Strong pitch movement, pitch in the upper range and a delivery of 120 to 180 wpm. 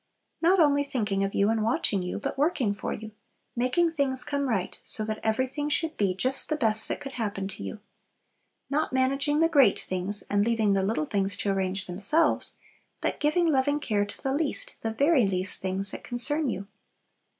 No: wide, 6.2 semitones; high, 230 Hz; average, 195 wpm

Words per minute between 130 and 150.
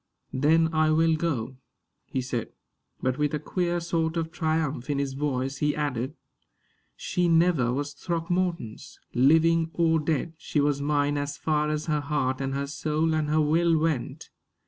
No: average, 165 wpm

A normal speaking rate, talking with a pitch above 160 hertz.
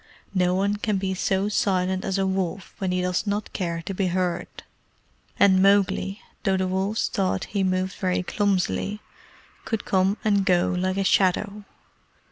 Yes: average, 165 wpm; high, 190 Hz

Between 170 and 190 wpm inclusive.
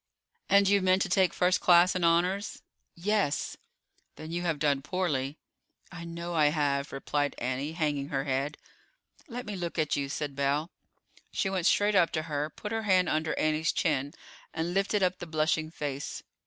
Yes: average, 180 wpm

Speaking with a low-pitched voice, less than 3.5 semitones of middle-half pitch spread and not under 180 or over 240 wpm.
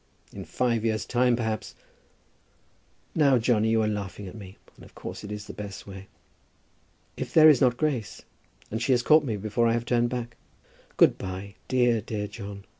Yes: low, 115 Hz; average, 2.9 semitones; average, 190 wpm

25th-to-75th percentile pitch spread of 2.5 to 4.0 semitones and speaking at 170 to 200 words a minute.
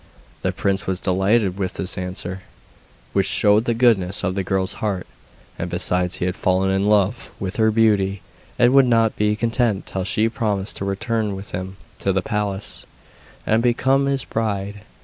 Yes: average, 2.8 semitones; average, 175 wpm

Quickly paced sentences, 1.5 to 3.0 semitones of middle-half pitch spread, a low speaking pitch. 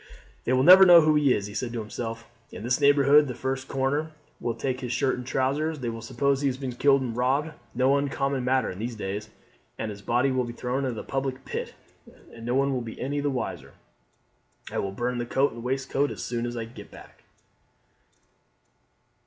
Yes: fast, 210 wpm; narrow, 2.6 semitones; low, 130 Hz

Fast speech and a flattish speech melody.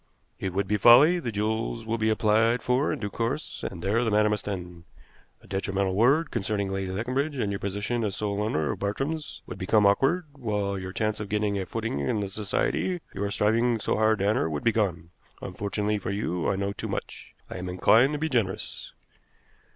No: fast, 210 wpm; average, 3.0 semitones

